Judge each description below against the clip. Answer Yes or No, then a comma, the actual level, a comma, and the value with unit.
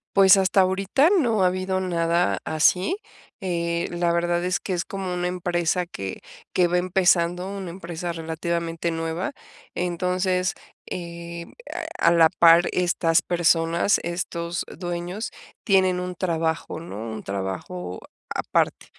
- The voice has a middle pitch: Yes, medium, 175 Hz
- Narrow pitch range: Yes, narrow, 1.5 semitones